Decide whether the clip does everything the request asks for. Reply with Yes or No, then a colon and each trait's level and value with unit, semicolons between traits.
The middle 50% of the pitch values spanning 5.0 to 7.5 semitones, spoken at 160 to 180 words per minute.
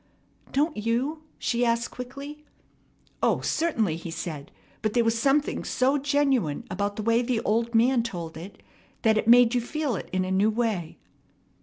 No: average, 4.4 semitones; average, 170 wpm